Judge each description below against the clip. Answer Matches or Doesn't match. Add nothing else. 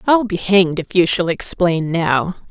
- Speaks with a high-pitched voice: Doesn't match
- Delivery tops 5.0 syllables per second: Doesn't match